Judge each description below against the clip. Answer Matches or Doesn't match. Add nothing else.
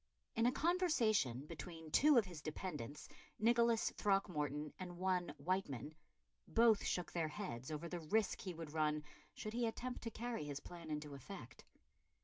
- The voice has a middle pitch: Matches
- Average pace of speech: Matches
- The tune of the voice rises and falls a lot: Matches